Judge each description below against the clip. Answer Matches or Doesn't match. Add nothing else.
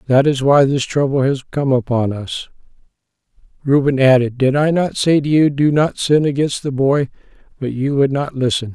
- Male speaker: Matches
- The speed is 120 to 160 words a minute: Doesn't match